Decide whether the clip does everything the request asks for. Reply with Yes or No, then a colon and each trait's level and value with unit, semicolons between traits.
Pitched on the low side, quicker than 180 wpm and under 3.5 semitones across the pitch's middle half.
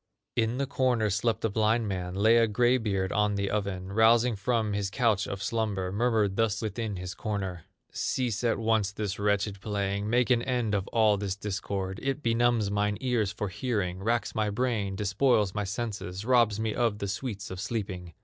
Yes: low, 105 Hz; average, 190 wpm; average, 2.8 semitones